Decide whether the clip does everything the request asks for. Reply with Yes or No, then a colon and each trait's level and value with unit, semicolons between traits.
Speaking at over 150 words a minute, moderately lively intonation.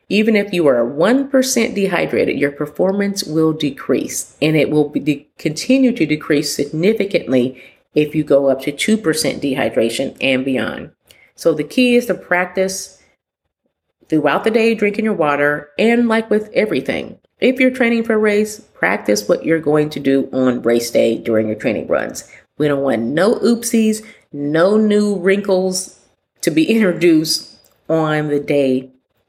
No: average, 160 wpm; wide, 6.7 semitones